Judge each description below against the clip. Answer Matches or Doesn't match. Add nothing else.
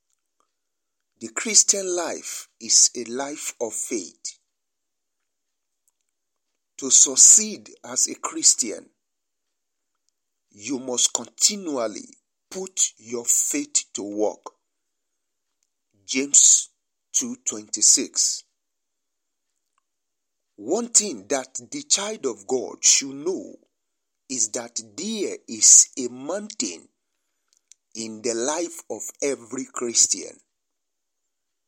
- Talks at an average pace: Doesn't match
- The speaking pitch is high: Matches